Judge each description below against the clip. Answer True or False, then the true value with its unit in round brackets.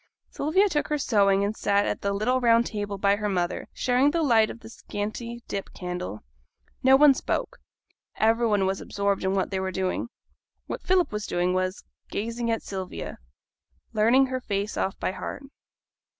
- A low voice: False (210 Hz)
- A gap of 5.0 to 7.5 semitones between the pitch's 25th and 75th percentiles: False (3.8 semitones)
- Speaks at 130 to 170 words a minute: False (180 wpm)